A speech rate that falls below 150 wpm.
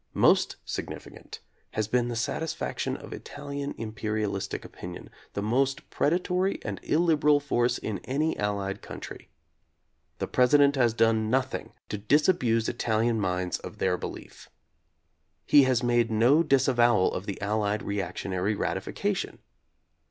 Yes: slow, 135 wpm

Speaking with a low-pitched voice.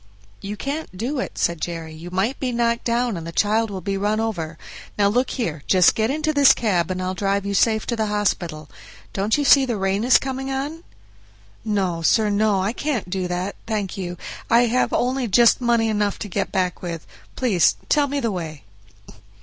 No: high, 210 Hz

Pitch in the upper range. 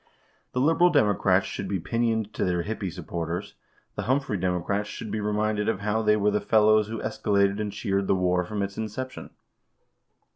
No: low, 105 Hz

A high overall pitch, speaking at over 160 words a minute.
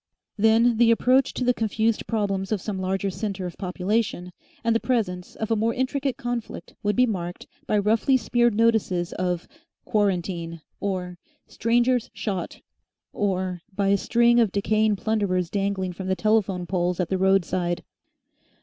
No: high, 205 Hz; average, 155 wpm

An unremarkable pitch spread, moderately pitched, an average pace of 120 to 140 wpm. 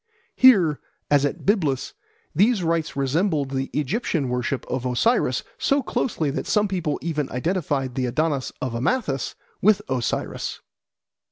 No: wide, 6.3 semitones; medium, 150 Hz; slow, 135 wpm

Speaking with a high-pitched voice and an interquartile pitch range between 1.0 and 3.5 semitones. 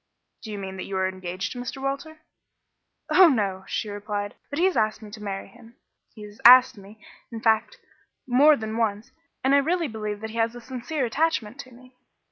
No: high, 225 Hz; average, 4.3 semitones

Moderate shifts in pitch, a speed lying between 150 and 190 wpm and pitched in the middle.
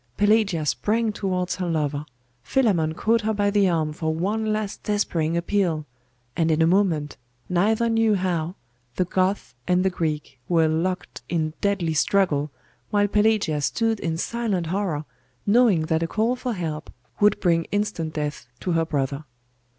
Yes: average, 4.5 semitones; average, 160 wpm; medium, 180 Hz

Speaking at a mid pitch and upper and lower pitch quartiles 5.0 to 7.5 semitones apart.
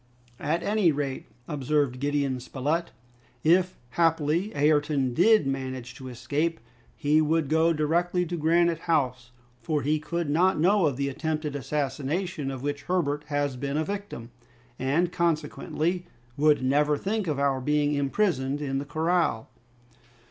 No: medium, 150 Hz; average, 3.4 semitones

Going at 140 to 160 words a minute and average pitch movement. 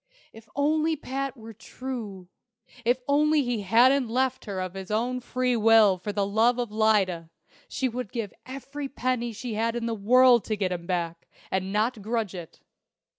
No: average, 175 wpm; average, 3.9 semitones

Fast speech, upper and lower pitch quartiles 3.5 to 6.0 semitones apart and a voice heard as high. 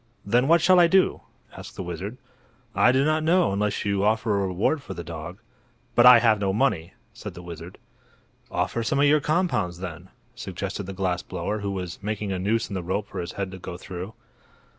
No: fast, 210 wpm; average, 5.1 semitones; low, 100 Hz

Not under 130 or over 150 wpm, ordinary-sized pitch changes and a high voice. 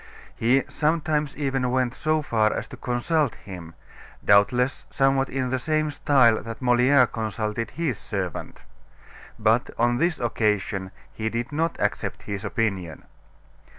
No: slow, 135 wpm; average, 4.3 semitones; low, 120 Hz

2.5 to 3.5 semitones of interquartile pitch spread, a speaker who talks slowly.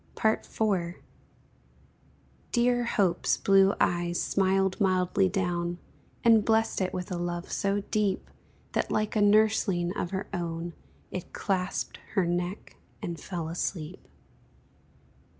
Yes: average, 2.8 semitones; slow, 115 wpm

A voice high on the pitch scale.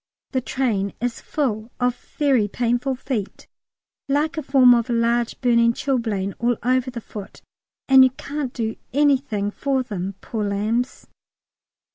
Yes: high, 245 Hz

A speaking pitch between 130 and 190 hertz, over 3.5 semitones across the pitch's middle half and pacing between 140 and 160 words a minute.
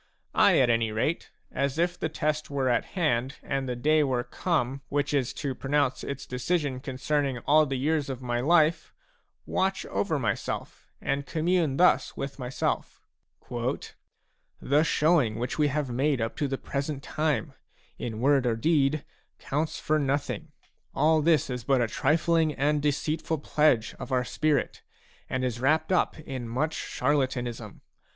No: medium, 140 Hz; average, 3.2 semitones; average, 155 wpm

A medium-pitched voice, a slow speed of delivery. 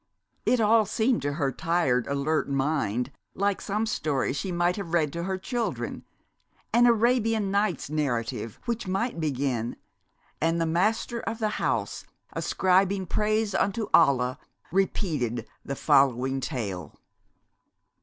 Yes: medium, 170 Hz; slow, 130 wpm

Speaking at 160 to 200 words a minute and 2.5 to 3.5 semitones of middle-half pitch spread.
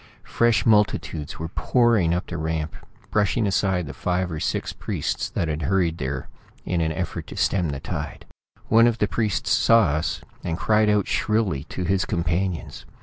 No: average, 175 wpm; average, 4.5 semitones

